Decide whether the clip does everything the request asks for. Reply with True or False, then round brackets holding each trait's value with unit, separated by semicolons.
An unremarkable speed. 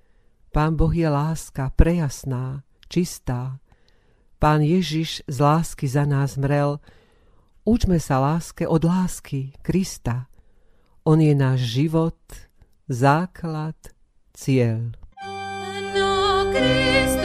False (85 wpm)